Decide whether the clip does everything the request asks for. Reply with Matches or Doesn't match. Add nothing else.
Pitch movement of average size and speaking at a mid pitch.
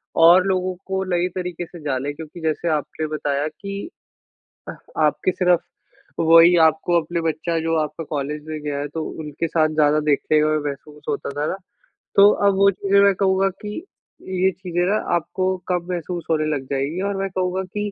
Matches